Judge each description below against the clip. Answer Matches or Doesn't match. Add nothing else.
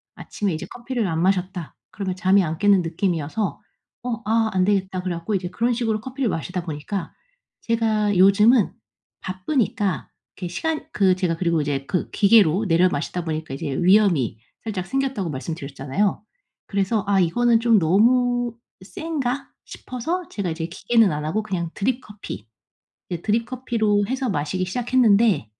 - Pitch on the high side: Matches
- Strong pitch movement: Doesn't match